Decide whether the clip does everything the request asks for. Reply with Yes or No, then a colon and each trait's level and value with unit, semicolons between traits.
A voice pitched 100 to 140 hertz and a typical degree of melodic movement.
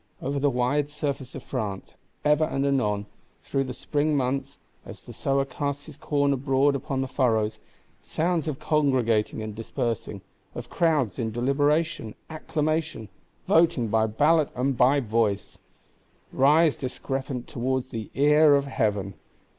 Yes: low, 135 Hz; average, 3.8 semitones